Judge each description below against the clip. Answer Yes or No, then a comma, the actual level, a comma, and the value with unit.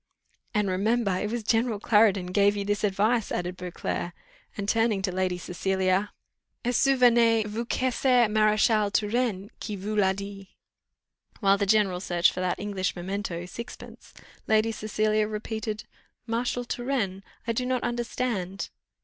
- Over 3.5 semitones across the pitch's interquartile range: No, average, 3.1 semitones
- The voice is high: Yes, high, 210 Hz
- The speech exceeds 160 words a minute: No, average, 150 wpm